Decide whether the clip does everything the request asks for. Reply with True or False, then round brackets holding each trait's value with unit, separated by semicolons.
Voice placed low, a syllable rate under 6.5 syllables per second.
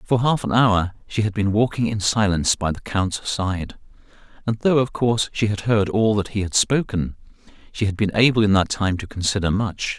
True (105 Hz; 5.2 syllables/s)